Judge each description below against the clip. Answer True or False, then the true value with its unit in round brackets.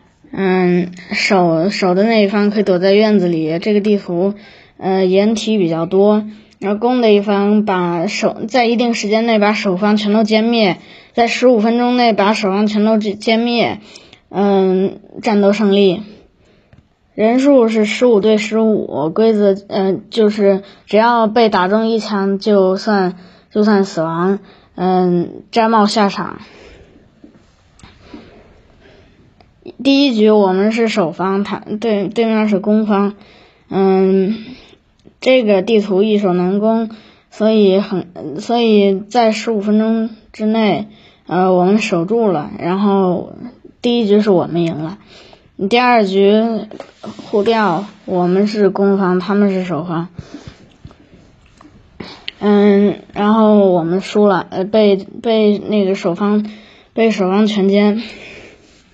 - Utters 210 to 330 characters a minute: False (185 characters per minute)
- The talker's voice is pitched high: True (205 Hz)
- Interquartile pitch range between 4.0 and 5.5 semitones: False (2.4 semitones)